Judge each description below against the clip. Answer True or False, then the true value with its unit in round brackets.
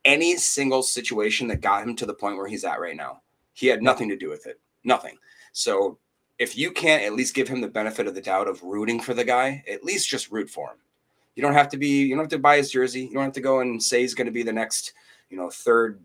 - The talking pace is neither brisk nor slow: False (275 wpm)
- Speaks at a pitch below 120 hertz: False (130 Hz)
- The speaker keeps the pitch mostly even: False (3.2 semitones)